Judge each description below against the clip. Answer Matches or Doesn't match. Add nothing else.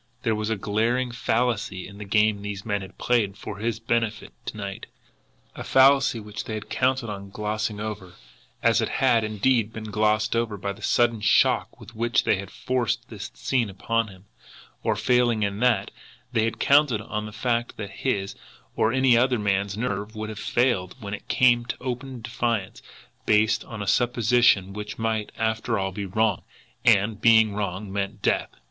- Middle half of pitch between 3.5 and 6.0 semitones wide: Doesn't match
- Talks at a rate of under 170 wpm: Doesn't match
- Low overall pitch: Matches